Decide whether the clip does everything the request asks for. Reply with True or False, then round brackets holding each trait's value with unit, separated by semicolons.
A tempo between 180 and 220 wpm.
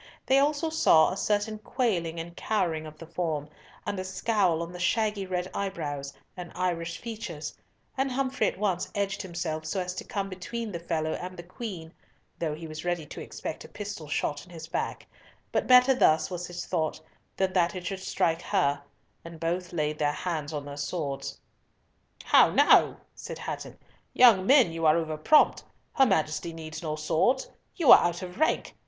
True (185 wpm)